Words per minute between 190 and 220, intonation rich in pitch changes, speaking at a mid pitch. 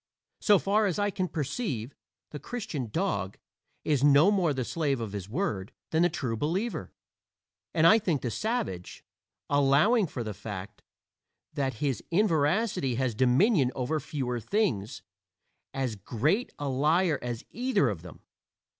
No: average, 145 wpm; wide, 7.6 semitones; medium, 145 Hz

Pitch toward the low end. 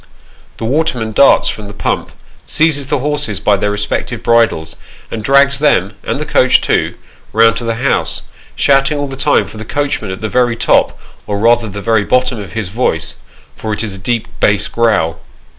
Yes: low, 115 Hz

